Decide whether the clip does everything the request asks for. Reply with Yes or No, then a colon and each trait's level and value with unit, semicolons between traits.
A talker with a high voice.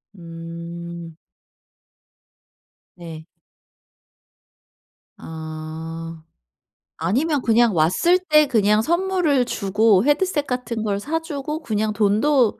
Yes: high, 215 Hz